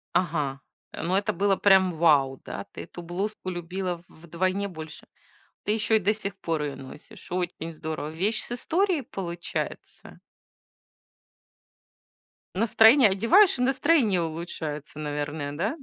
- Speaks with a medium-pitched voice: Yes, medium, 180 Hz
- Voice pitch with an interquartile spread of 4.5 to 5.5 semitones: Yes, average, 5.0 semitones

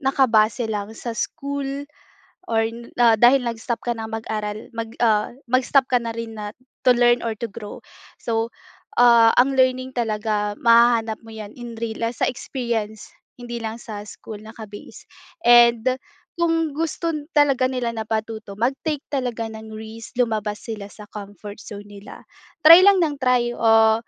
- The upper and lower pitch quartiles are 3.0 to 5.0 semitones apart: No, narrow, 2.4 semitones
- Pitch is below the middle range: No, high, 230 Hz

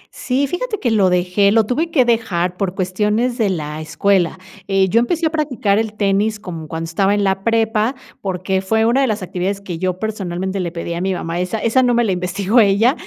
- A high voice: Yes, high, 200 Hz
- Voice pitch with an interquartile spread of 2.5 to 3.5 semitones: No, average, 3.9 semitones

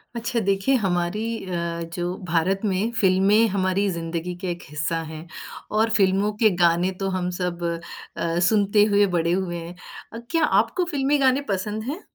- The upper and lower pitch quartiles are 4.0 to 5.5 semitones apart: No, average, 3.5 semitones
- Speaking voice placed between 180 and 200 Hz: Yes, high, 190 Hz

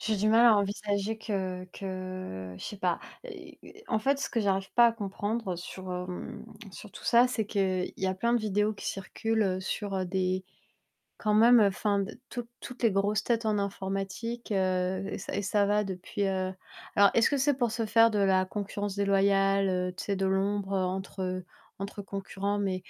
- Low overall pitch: No, high, 200 Hz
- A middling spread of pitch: No, narrow, 2.3 semitones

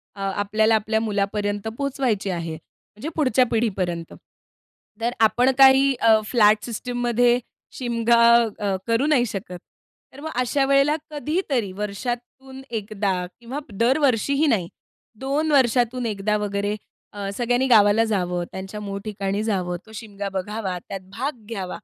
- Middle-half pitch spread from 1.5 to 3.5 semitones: No, average, 4.0 semitones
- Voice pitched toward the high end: Yes, high, 225 Hz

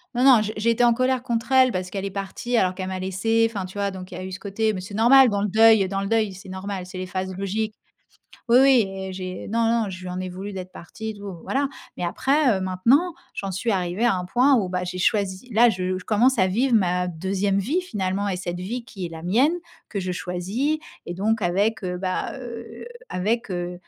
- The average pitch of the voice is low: No, high, 195 Hz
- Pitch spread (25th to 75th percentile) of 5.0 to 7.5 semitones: No, average, 3.7 semitones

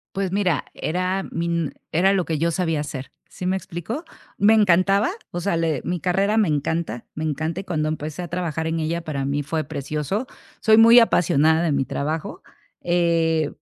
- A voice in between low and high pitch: Yes, medium, 165 Hz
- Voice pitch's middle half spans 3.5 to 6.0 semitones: No, average, 3.1 semitones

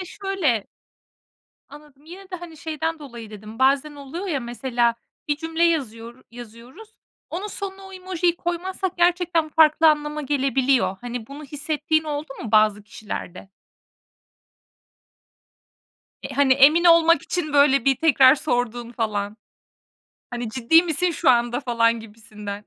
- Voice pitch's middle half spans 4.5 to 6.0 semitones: Yes, wide, 5.6 semitones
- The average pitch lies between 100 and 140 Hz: No, very high, 285 Hz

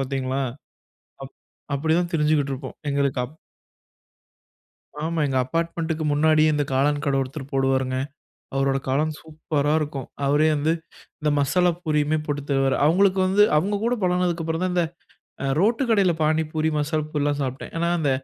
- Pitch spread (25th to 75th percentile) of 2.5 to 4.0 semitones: Yes, average, 3.0 semitones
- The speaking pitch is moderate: Yes, medium, 155 Hz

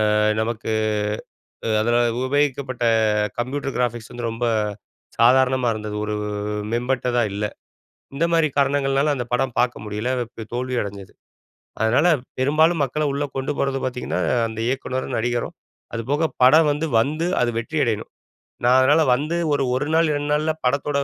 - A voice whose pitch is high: No, low, 130 Hz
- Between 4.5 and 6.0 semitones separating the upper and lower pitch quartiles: No, average, 3.3 semitones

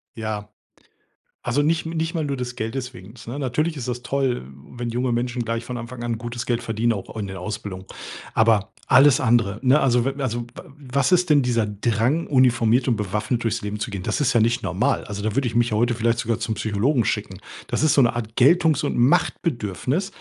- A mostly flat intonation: No, average, 3.2 semitones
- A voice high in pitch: No, low, 120 Hz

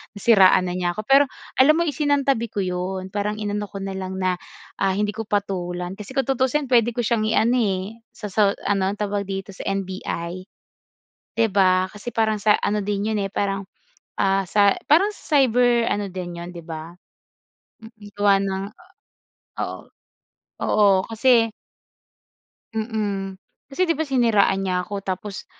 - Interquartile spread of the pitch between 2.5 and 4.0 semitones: Yes, average, 3.3 semitones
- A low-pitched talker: No, high, 205 Hz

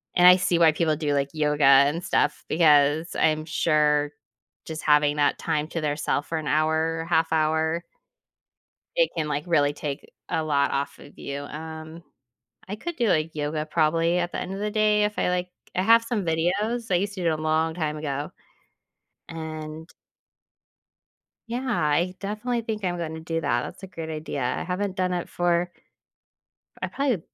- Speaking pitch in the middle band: Yes, medium, 160 Hz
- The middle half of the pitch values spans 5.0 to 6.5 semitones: No, average, 3.0 semitones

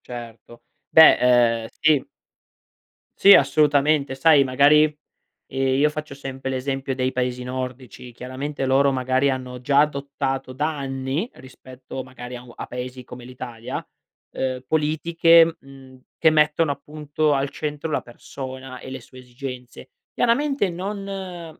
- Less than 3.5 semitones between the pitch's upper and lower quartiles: Yes, average, 2.9 semitones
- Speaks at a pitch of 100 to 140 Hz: Yes, low, 135 Hz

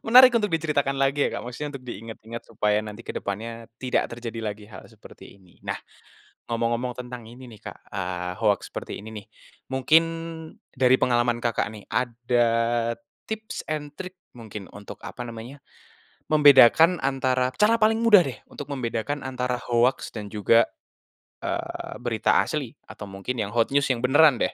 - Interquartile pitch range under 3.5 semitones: No, average, 3.9 semitones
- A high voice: No, low, 120 Hz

